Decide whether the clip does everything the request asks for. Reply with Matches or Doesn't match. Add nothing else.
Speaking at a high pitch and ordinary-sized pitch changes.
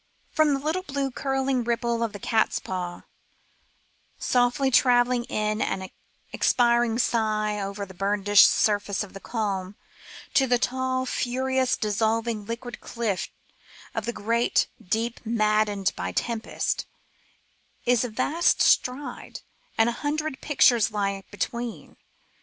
Matches